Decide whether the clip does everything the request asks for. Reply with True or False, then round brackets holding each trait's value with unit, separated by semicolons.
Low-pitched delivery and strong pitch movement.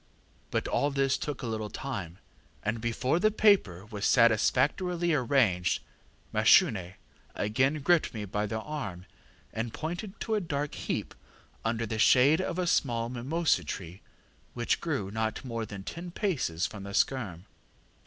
True (120 Hz; 6.5 semitones)